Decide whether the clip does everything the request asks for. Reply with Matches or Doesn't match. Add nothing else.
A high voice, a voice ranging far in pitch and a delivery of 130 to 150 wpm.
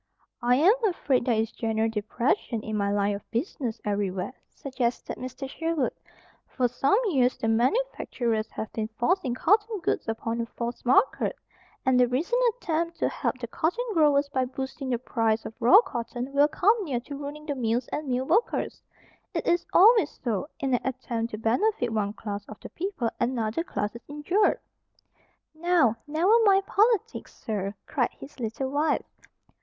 Doesn't match